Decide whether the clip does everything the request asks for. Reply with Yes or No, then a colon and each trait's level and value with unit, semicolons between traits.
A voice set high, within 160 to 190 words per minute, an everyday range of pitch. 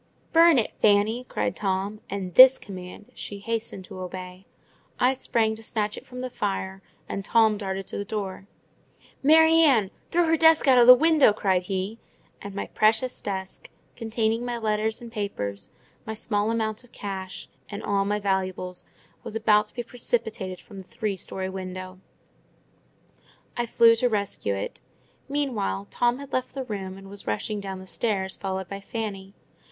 Yes: high, 210 Hz; average, 170 wpm; average, 3.5 semitones